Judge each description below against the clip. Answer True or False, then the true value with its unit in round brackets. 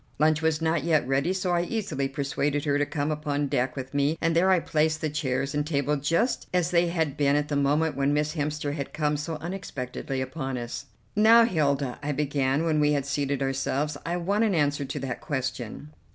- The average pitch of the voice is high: False (150 Hz)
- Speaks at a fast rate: True (210 wpm)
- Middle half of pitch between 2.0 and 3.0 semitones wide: True (2.6 semitones)